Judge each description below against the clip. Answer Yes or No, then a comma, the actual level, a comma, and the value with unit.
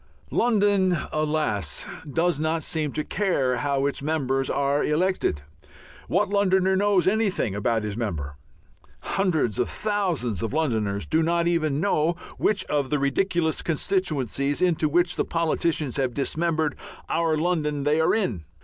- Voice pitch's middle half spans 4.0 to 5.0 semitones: Yes, average, 4.7 semitones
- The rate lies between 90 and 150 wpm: Yes, average, 140 wpm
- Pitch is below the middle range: No, medium, 155 Hz